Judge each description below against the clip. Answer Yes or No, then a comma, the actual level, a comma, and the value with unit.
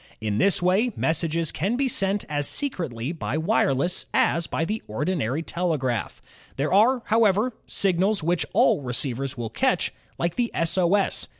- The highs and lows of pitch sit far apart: Yes, wide, 6.1 semitones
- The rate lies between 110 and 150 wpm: No, average, 160 wpm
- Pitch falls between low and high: Yes, medium, 170 Hz